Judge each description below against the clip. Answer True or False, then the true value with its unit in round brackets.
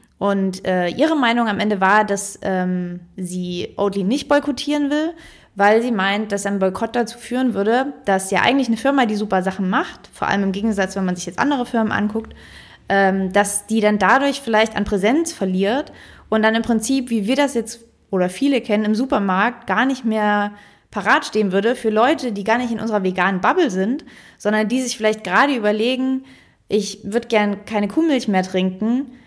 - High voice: True (215 Hz)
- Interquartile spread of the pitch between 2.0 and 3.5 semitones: False (4.0 semitones)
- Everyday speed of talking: False (195 wpm)